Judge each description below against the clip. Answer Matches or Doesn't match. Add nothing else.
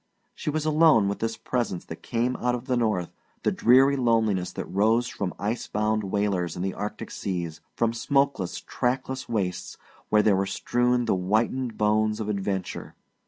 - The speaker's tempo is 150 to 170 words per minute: Matches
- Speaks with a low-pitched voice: Matches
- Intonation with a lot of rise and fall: Doesn't match